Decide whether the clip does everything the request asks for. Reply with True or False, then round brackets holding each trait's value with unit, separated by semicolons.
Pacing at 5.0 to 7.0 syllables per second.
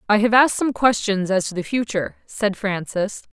True (5.4 syllables/s)